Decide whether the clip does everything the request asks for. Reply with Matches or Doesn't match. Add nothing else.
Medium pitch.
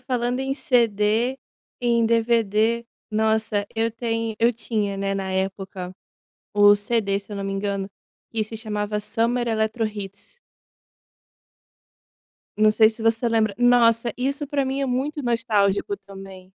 Doesn't match